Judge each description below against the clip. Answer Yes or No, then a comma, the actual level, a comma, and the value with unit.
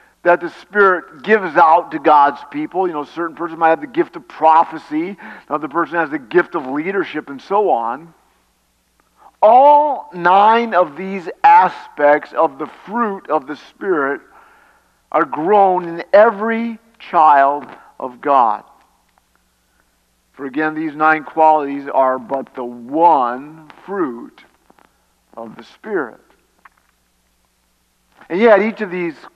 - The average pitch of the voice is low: No, medium, 165 Hz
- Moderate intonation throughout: No, wide, 6.6 semitones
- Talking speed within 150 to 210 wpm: No, slow, 135 wpm